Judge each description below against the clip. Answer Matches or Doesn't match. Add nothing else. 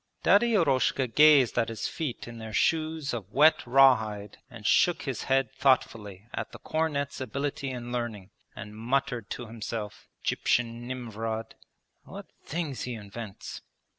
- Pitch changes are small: Doesn't match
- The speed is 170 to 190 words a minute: Doesn't match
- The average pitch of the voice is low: Matches